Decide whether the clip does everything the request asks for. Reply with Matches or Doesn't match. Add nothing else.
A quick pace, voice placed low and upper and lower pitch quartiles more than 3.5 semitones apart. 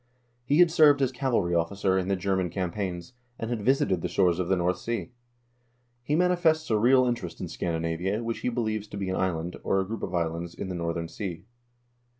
Matches